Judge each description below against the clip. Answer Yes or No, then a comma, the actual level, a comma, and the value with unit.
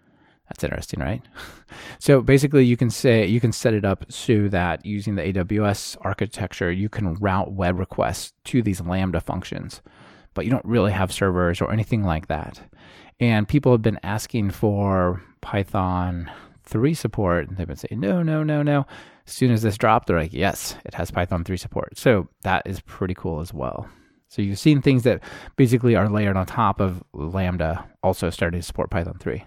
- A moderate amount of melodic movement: Yes, average, 4.1 semitones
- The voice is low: Yes, low, 100 Hz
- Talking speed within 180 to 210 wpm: Yes, average, 190 wpm